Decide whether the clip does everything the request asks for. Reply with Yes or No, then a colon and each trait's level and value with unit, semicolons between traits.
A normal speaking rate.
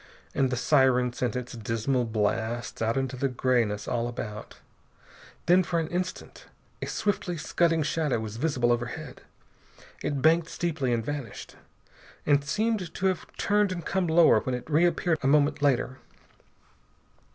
Yes: average, 150 wpm